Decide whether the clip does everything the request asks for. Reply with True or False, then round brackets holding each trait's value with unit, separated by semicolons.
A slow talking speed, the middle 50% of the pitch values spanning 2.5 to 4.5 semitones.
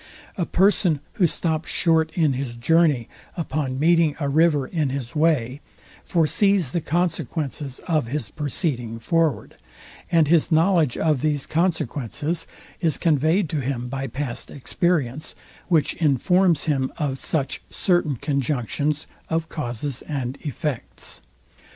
True (125 wpm; 3.7 semitones)